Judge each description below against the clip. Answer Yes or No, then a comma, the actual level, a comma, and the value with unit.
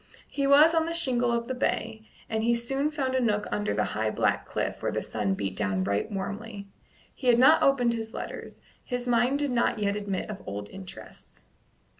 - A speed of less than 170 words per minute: No, fast, 205 wpm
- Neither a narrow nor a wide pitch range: Yes, average, 4.5 semitones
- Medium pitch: No, high, 235 Hz